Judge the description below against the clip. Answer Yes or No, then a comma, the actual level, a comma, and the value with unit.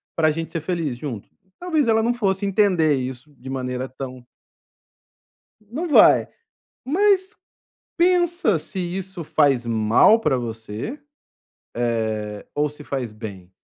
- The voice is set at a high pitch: No, medium, 155 Hz